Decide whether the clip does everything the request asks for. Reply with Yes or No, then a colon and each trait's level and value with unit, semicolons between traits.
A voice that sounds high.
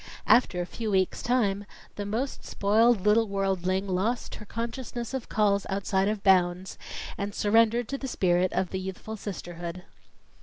Yes: high, 200 Hz